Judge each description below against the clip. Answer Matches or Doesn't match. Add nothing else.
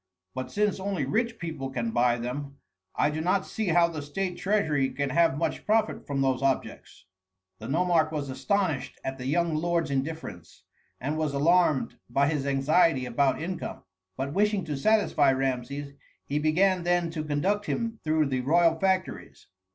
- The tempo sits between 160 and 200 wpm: Matches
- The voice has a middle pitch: Matches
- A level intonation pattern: Doesn't match